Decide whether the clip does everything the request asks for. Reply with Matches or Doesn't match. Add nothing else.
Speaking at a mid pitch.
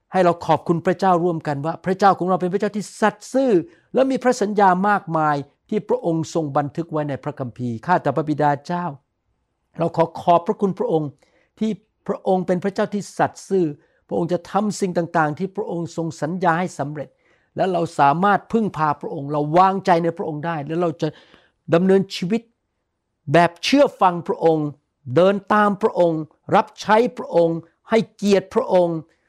Matches